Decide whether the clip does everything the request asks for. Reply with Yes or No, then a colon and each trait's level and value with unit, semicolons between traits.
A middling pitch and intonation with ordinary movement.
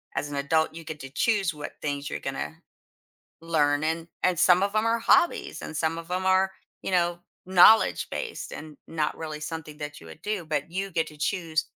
Yes: medium, 165 Hz; average, 3.6 semitones